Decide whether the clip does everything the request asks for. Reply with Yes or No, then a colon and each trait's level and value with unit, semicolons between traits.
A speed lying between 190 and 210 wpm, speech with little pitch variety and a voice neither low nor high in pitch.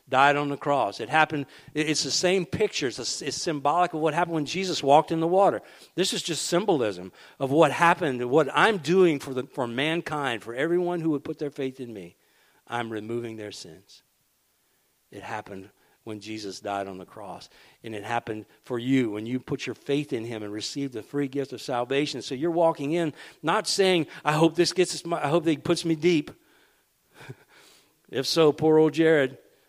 No: average, 200 wpm; average, 5.0 semitones; medium, 145 Hz